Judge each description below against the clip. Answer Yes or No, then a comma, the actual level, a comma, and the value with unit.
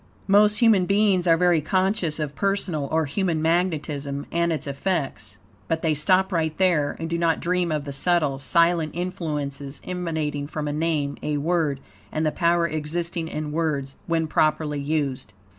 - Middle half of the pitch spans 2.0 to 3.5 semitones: Yes, average, 3.0 semitones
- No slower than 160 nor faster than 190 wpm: Yes, average, 165 wpm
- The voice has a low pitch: No, medium, 160 Hz